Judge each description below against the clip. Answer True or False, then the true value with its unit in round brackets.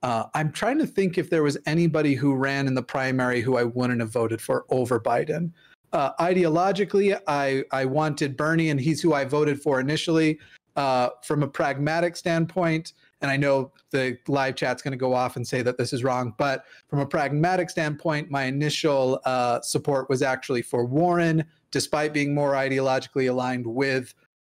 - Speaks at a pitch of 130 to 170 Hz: True (140 Hz)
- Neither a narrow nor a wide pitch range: True (3.5 semitones)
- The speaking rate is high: False (185 wpm)